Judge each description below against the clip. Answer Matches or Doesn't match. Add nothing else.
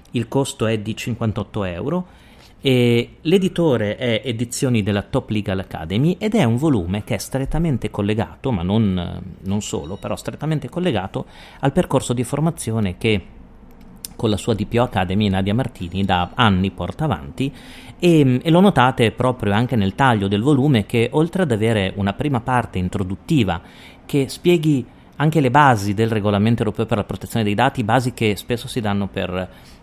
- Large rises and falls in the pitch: Doesn't match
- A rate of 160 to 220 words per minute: Matches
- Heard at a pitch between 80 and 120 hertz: Matches